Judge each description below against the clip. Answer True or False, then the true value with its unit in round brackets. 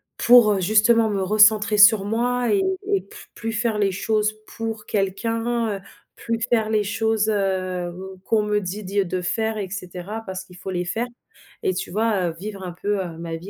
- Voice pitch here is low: False (210 Hz)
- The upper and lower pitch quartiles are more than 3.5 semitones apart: False (2.9 semitones)